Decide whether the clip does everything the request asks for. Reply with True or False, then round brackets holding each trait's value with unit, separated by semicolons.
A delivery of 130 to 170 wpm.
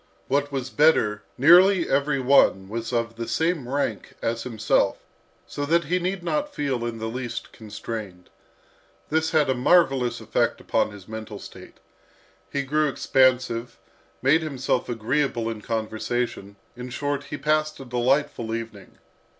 True (145 wpm)